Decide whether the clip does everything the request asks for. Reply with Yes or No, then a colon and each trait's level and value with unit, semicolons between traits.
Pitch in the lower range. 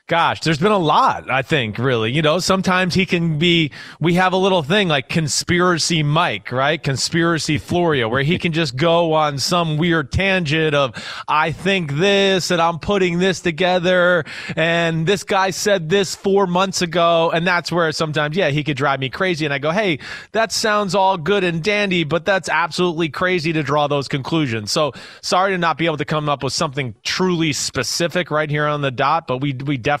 No: medium, 165 Hz